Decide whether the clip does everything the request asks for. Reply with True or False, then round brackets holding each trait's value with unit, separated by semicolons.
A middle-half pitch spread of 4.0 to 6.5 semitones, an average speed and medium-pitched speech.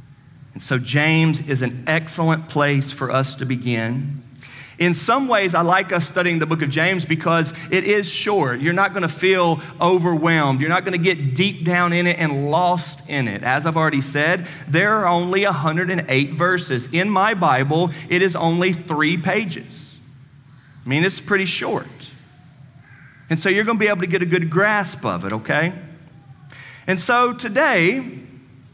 True (4.5 semitones; 170 wpm; 160 Hz)